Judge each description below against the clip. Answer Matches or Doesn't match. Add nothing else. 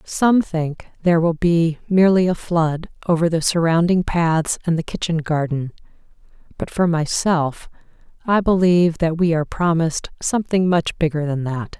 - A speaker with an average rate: Matches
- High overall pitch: Doesn't match